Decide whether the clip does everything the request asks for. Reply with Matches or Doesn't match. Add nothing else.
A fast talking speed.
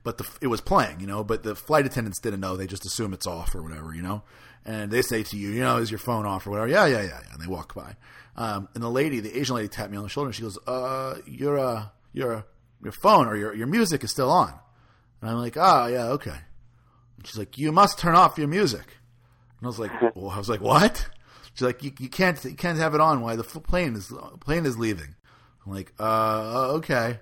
Matches